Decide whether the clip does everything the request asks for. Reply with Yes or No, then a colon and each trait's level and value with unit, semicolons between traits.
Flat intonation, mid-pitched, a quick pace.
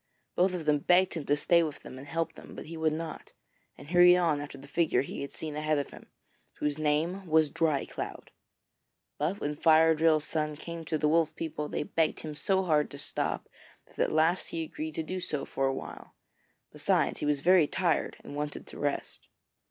Yes: narrow, 2.1 semitones; medium, 155 Hz; fast, 215 wpm